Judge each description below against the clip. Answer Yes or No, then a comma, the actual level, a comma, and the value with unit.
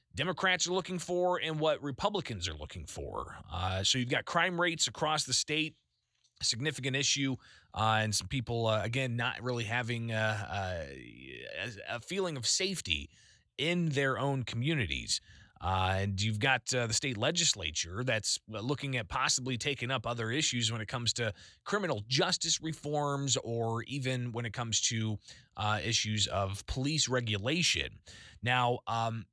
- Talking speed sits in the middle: Yes, average, 160 wpm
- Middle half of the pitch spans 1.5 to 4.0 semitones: No, average, 5.0 semitones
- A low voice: Yes, low, 120 Hz